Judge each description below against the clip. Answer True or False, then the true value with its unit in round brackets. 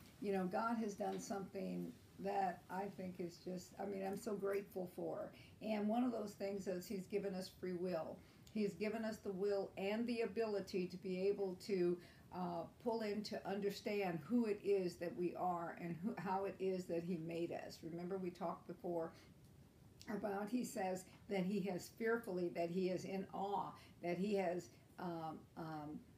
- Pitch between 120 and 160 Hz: False (190 Hz)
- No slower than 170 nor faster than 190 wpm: True (185 wpm)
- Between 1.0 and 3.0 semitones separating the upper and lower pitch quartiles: True (2.4 semitones)